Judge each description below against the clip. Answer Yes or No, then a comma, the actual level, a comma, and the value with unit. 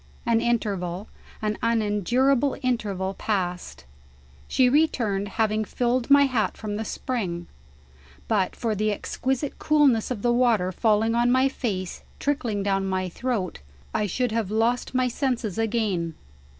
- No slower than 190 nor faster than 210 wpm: No, slow, 135 wpm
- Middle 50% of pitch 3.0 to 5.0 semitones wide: Yes, average, 4.0 semitones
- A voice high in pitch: Yes, high, 225 Hz